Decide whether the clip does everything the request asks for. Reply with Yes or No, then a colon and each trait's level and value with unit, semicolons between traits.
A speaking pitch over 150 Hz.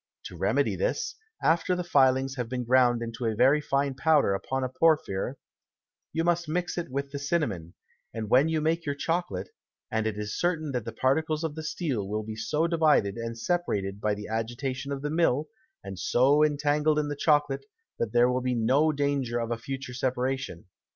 No: low, 135 Hz